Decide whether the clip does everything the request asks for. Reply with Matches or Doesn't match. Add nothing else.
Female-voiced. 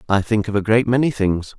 Doesn't match